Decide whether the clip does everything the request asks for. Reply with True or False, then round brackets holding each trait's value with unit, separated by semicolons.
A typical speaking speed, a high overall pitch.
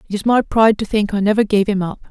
False (315 wpm; 205 Hz)